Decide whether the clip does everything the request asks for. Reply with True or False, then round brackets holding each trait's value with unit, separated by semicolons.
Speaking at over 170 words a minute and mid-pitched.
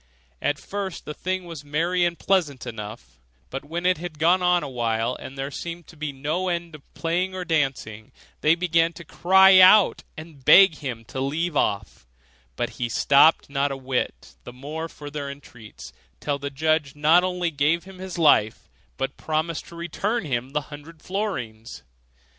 True (180 wpm; 155 Hz)